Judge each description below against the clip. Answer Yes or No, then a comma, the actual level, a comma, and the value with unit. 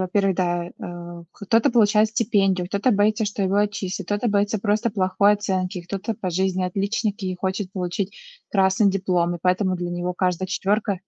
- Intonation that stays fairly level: Yes, narrow, 2.2 semitones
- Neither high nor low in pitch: No, high, 195 Hz